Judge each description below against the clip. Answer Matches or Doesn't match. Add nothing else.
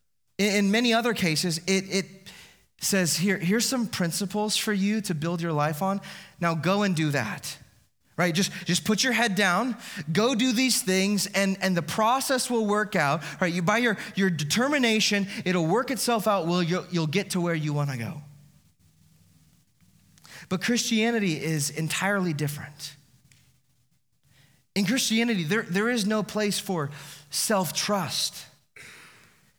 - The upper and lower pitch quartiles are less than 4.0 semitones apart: Doesn't match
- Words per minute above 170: Doesn't match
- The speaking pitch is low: Doesn't match